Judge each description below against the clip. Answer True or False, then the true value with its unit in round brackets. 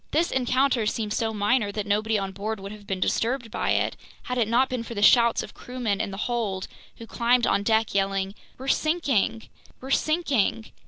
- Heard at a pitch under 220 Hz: False (225 Hz)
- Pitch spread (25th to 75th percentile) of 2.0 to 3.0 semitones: False (3.6 semitones)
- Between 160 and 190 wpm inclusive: False (200 wpm)